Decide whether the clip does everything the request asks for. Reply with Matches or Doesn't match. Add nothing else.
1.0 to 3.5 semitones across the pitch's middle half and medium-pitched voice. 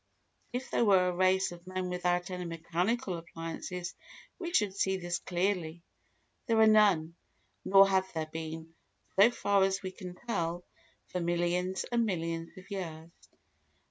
Matches